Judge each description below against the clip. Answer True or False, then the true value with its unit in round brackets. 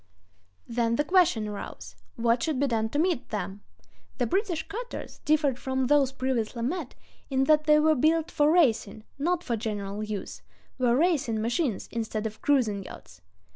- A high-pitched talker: True (255 Hz)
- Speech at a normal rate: True (160 wpm)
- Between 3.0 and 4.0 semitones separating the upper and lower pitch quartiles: False (5.6 semitones)